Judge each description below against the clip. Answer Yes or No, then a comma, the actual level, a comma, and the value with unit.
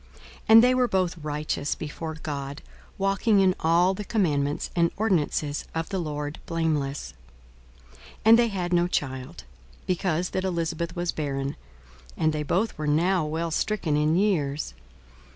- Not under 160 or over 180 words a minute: No, average, 150 wpm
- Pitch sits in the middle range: Yes, medium, 165 Hz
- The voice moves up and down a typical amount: Yes, average, 4.0 semitones